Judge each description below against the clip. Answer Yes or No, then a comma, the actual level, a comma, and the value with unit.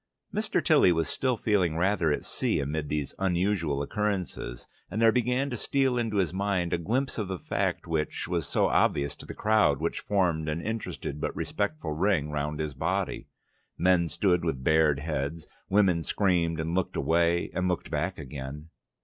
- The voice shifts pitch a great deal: No, average, 4.9 semitones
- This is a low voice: Yes, very low, 85 Hz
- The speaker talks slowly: No, average, 175 wpm